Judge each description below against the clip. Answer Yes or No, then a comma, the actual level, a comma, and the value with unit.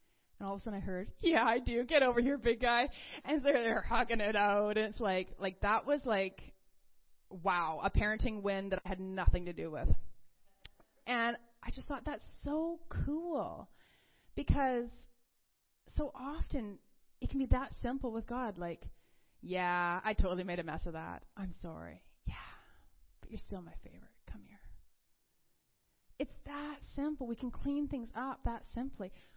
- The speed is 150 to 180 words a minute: Yes, average, 170 wpm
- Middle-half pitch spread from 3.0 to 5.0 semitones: No, wide, 5.6 semitones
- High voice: Yes, high, 230 Hz